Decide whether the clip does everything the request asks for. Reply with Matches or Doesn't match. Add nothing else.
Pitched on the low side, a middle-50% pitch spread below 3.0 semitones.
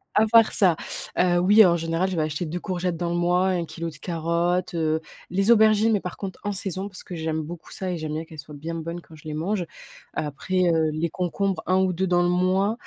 Doesn't match